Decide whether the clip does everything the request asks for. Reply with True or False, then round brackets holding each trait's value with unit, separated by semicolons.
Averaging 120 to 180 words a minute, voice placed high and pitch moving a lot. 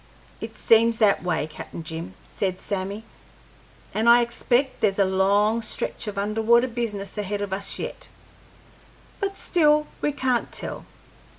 False (140 wpm; 210 Hz; 3.4 semitones)